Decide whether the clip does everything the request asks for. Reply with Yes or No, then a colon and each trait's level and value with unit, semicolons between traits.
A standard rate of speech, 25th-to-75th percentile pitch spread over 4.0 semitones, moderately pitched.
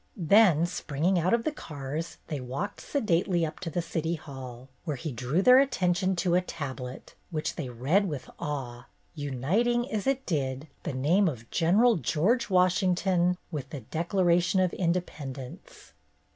Yes: average, 155 wpm; average, 5.1 semitones; medium, 170 Hz